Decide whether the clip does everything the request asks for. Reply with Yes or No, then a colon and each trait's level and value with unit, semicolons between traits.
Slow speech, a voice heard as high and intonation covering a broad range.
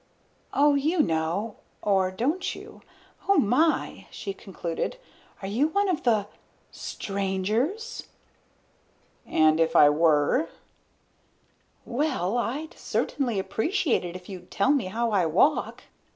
Yes: slow, 120 wpm; high, 215 Hz; wide, 8.1 semitones